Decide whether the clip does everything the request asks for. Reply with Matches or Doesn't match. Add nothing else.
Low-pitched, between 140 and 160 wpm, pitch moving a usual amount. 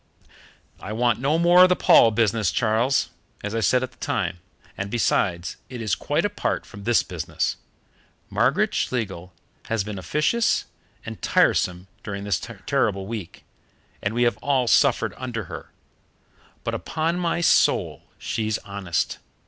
Matches